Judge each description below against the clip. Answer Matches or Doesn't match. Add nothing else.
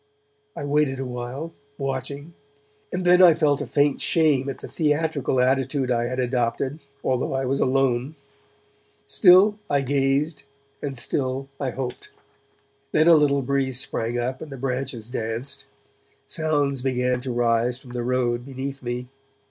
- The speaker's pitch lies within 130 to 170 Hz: Matches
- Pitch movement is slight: Matches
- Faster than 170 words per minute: Doesn't match